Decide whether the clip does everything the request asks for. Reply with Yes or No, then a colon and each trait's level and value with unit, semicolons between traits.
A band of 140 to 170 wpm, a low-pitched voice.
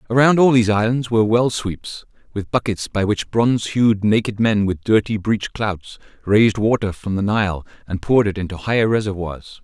No: average, 185 wpm; low, 105 Hz